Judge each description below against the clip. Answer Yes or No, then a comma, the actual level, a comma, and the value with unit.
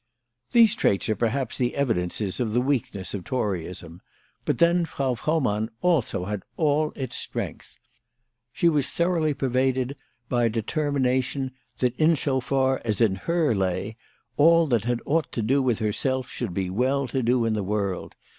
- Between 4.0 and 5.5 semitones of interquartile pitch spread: Yes, average, 4.9 semitones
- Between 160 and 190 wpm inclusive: Yes, average, 170 wpm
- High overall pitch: No, low, 125 Hz